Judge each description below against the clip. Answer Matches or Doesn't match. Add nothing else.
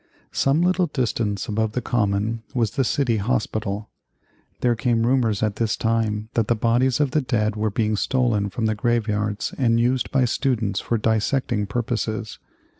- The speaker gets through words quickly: Doesn't match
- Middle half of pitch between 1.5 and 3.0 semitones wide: Matches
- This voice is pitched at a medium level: Doesn't match